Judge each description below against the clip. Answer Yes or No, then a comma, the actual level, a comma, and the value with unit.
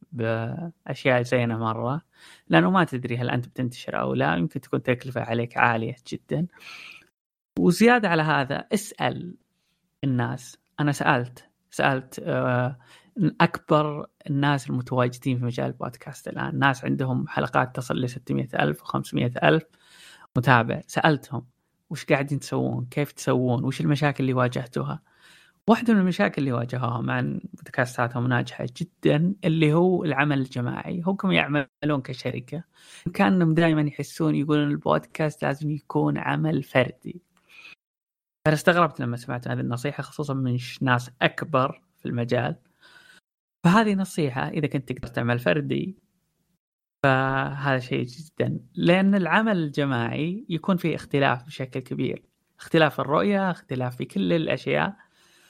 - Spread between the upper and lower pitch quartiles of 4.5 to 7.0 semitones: Yes, average, 4.9 semitones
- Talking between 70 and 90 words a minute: No, average, 120 wpm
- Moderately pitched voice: Yes, medium, 145 Hz